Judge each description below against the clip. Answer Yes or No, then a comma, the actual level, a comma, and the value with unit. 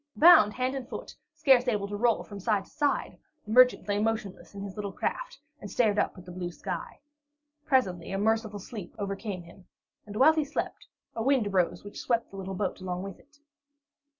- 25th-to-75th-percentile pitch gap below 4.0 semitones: No, average, 4.3 semitones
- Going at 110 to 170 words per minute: No, fast, 205 wpm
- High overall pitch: Yes, high, 210 Hz